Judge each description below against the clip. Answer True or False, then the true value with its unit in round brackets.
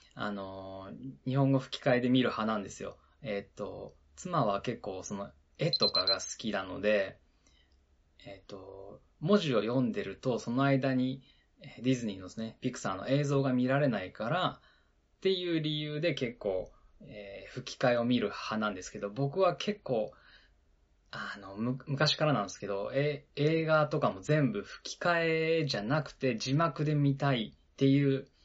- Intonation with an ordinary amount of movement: False (6.2 semitones)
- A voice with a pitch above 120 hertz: True (130 Hz)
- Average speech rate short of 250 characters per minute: False (300 characters per minute)